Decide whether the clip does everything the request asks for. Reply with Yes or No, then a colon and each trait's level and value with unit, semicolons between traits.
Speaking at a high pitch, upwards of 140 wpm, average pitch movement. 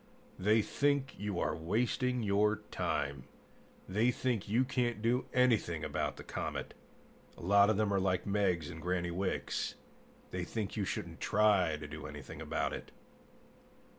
No: low, 100 Hz; average, 155 wpm; average, 4.5 semitones